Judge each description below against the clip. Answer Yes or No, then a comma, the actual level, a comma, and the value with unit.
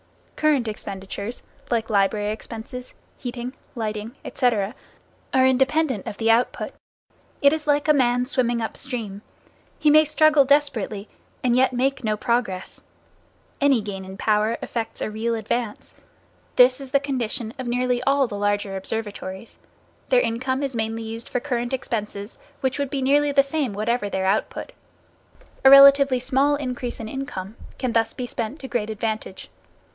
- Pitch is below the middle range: No, high, 240 Hz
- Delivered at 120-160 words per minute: Yes, average, 155 wpm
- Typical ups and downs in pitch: Yes, average, 3.8 semitones